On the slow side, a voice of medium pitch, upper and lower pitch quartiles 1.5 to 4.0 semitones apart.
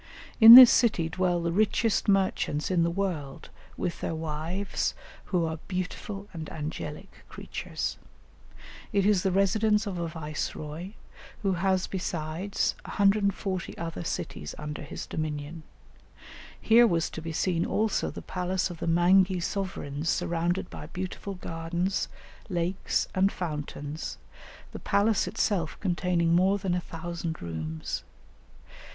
Yes: slow, 130 wpm; medium, 180 Hz; average, 3.2 semitones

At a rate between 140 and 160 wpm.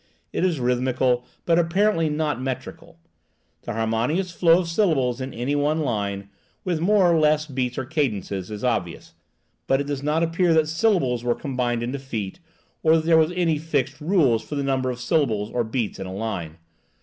No: average, 185 wpm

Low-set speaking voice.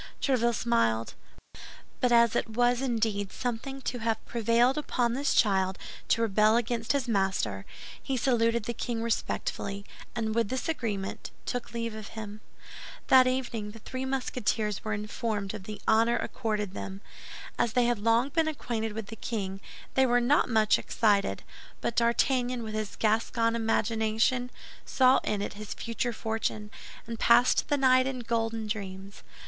No: high, 230 Hz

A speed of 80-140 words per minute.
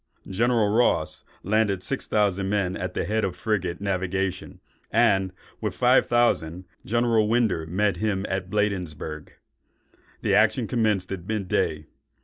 Yes: slow, 135 wpm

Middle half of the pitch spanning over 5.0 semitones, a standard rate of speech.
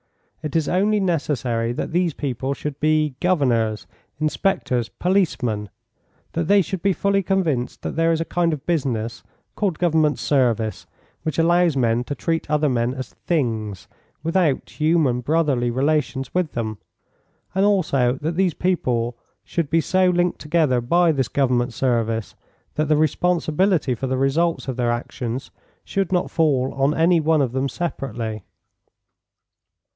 Yes: wide, 5.5 semitones; average, 150 wpm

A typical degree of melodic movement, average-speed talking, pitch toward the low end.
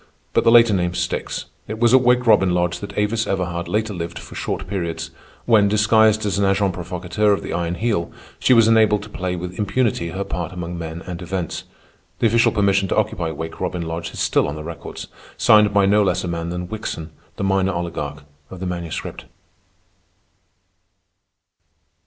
Yes: average, 3.5 semitones; average, 190 wpm; very low, 95 Hz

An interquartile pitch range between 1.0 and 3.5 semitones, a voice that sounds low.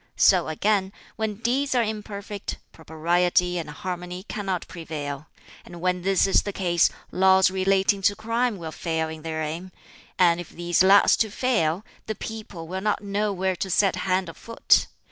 No: average, 3.1 semitones; medium, 185 Hz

